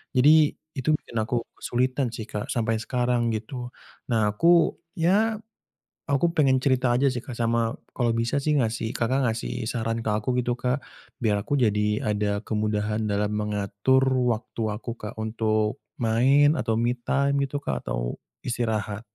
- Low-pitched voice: Yes, low, 120 Hz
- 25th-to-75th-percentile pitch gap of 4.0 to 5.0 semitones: No, average, 3.4 semitones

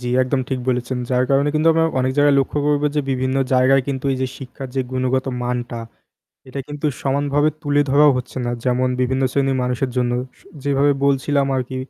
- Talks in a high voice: No, low, 135 Hz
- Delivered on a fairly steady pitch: Yes, narrow, 1.9 semitones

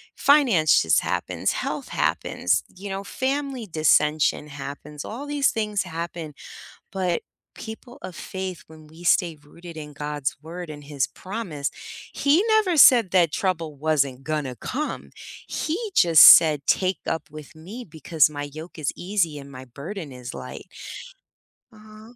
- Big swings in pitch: Yes, wide, 5.9 semitones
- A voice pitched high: No, medium, 165 Hz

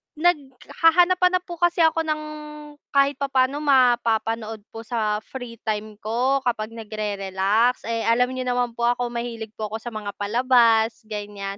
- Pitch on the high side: Yes, high, 235 Hz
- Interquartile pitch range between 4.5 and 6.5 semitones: No, average, 3.7 semitones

